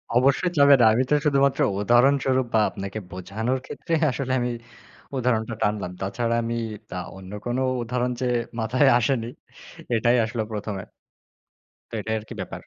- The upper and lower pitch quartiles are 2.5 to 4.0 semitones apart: Yes, average, 3.0 semitones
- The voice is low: Yes, low, 120 Hz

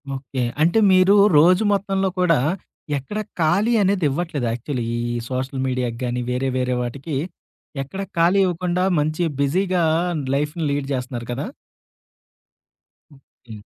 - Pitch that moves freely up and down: Yes, wide, 6.1 semitones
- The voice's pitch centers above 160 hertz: No, medium, 150 Hz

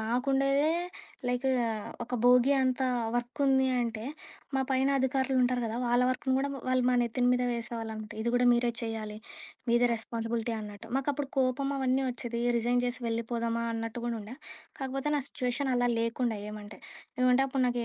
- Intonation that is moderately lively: No, narrow, 2.2 semitones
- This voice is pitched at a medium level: No, high, 245 Hz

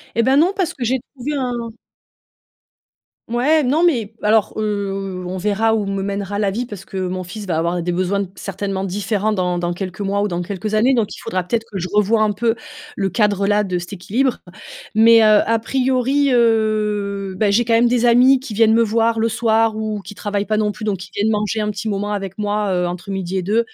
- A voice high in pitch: Yes, high, 210 Hz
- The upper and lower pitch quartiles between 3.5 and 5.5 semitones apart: No, average, 2.8 semitones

